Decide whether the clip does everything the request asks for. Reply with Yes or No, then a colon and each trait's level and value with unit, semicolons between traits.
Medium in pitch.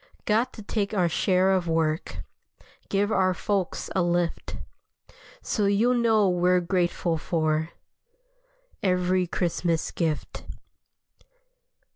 Yes: medium, 180 Hz